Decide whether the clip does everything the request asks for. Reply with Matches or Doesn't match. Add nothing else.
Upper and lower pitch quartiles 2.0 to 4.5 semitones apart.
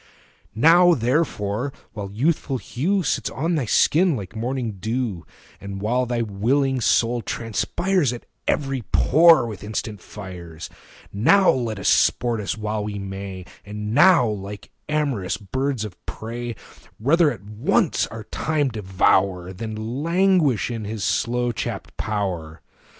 Doesn't match